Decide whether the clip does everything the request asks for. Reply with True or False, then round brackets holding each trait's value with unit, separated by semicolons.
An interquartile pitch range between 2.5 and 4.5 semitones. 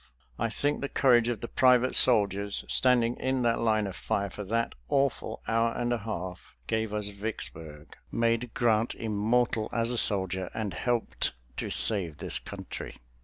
True (2.9 semitones)